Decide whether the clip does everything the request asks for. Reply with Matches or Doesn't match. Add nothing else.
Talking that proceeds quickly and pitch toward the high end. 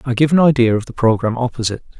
Doesn't match